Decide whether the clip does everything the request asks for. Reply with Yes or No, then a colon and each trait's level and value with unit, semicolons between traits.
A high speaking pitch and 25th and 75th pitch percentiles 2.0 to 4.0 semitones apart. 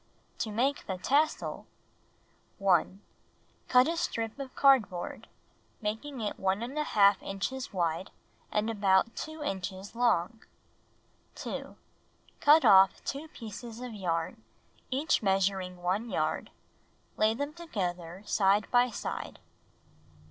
No: high, 215 Hz; average, 5.2 semitones